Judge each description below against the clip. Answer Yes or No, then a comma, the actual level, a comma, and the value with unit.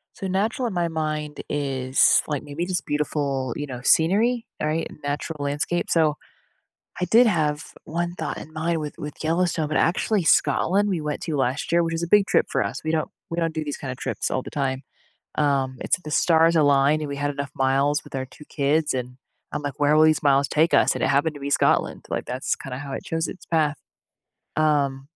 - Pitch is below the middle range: No, medium, 150 Hz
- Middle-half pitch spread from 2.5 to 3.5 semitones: Yes, average, 2.8 semitones